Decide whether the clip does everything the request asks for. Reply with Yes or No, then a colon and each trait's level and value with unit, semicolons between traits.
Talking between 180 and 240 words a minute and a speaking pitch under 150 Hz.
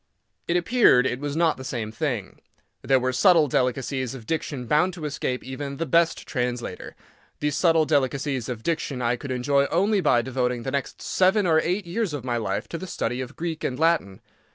Yes: average, 200 wpm; medium, 140 Hz